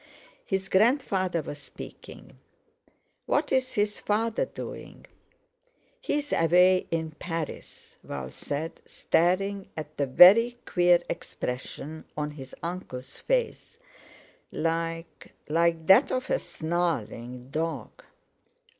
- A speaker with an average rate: No, slow, 95 wpm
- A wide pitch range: No, average, 4.4 semitones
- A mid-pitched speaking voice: Yes, medium, 170 Hz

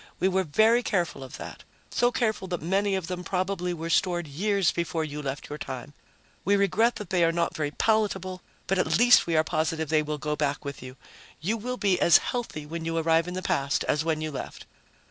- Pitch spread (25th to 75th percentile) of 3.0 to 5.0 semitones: Yes, average, 4.1 semitones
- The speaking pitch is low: No, medium, 170 Hz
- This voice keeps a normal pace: No, fast, 220 wpm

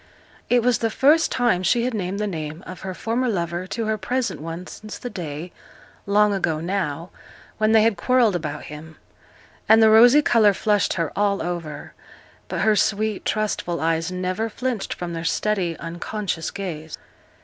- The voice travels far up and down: No, average, 4.5 semitones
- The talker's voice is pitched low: No, high, 195 Hz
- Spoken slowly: No, average, 170 wpm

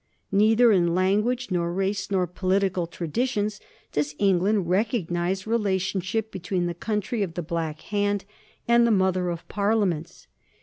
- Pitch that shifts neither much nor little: Yes, average, 3.2 semitones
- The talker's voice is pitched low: No, high, 190 Hz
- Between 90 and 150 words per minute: Yes, average, 140 wpm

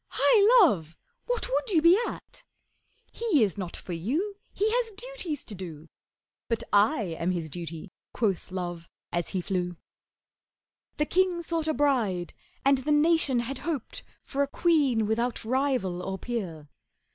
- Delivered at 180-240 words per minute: No, average, 155 wpm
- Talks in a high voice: Yes, high, 245 Hz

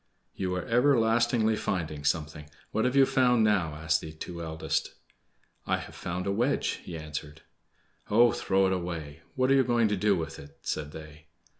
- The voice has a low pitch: Yes, very low, 90 Hz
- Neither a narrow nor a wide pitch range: No, wide, 6.7 semitones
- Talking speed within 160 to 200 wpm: Yes, average, 180 wpm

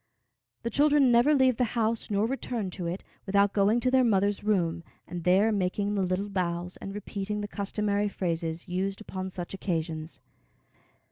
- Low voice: No, high, 200 Hz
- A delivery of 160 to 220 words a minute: Yes, average, 165 wpm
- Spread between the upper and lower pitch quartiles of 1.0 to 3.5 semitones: Yes, average, 3.1 semitones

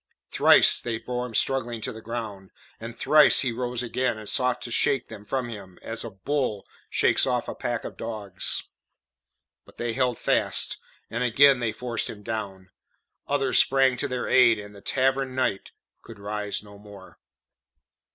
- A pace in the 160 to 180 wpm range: Yes, average, 170 wpm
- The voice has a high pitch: No, low, 115 Hz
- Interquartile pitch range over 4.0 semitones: No, average, 3.3 semitones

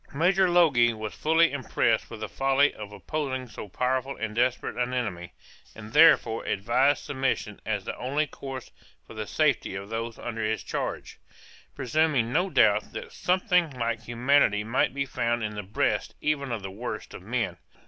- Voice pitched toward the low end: Yes, low, 125 Hz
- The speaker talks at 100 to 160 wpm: No, average, 170 wpm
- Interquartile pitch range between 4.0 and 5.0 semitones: Yes, average, 4.4 semitones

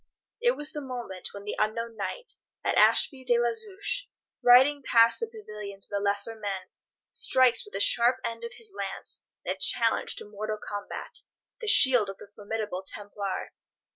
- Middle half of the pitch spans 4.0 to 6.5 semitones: Yes, average, 4.5 semitones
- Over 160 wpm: Yes, average, 175 wpm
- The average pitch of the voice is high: Yes, high, 230 Hz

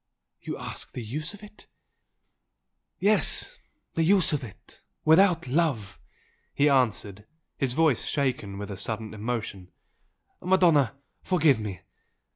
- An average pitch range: No, wide, 7.4 semitones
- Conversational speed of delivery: No, slow, 125 wpm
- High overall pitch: No, low, 135 Hz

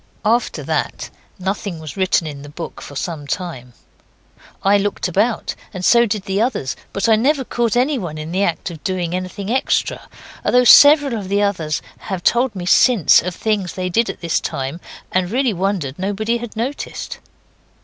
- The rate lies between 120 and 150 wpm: No, average, 180 wpm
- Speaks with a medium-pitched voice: No, high, 195 Hz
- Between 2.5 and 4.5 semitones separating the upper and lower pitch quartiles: No, average, 5.0 semitones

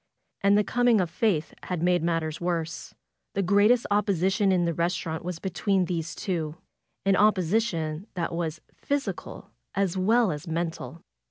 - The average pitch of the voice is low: No, medium, 180 Hz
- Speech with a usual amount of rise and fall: Yes, average, 3.3 semitones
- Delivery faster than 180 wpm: No, average, 160 wpm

